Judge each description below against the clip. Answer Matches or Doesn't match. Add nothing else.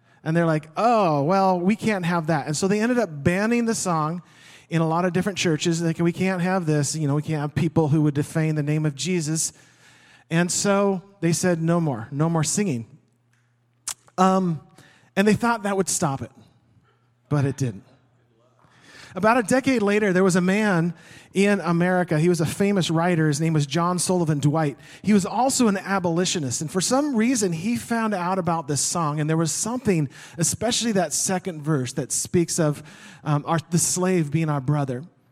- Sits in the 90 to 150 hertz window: Doesn't match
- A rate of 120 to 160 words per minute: Doesn't match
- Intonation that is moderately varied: Matches